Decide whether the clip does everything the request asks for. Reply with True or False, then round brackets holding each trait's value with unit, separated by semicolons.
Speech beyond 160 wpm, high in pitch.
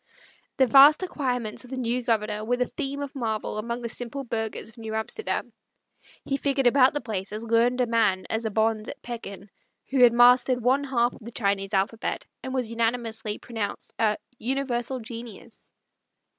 True (180 wpm; 235 Hz)